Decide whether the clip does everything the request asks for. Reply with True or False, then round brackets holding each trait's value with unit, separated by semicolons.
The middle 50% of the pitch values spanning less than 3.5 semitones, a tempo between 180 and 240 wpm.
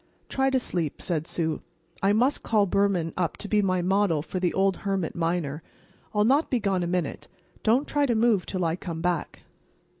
False (3.8 semitones; 200 wpm)